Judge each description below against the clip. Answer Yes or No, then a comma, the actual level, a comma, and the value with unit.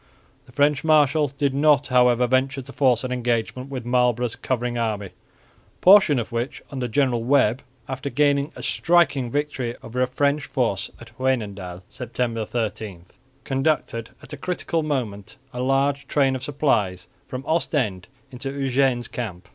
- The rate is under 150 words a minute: No, average, 155 wpm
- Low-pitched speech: Yes, low, 130 Hz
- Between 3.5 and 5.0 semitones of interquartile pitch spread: No, average, 3.1 semitones